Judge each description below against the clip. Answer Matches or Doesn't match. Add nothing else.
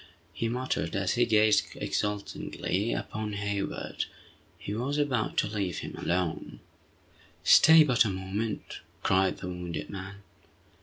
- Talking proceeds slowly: Matches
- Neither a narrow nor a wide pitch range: Matches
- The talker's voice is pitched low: Matches